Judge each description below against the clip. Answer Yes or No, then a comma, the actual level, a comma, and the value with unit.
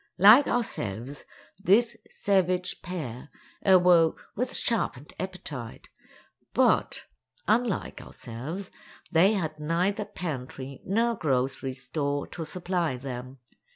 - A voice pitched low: No, medium, 170 Hz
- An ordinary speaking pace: No, slow, 95 wpm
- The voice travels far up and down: Yes, wide, 6.3 semitones